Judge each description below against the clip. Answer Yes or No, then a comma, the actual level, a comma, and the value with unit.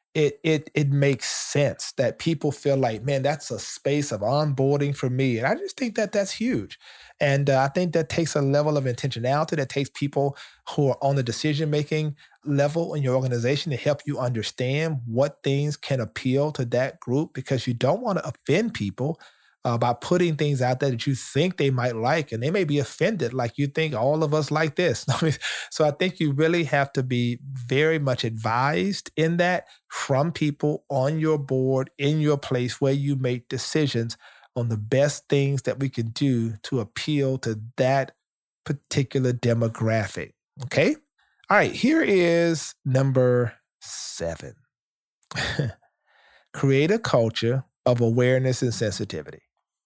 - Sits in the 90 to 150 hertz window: Yes, medium, 140 Hz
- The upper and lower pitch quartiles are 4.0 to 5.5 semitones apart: No, average, 3.4 semitones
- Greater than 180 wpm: No, average, 170 wpm